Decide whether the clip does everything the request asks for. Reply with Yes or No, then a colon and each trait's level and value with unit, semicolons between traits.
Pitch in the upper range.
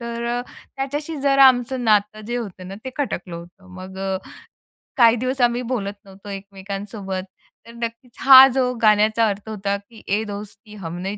Yes: high, 215 Hz